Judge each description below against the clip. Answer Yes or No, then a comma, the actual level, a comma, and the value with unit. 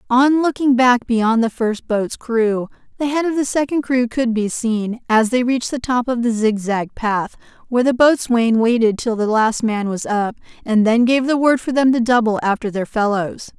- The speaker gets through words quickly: Yes, fast, 210 wpm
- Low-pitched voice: No, high, 235 Hz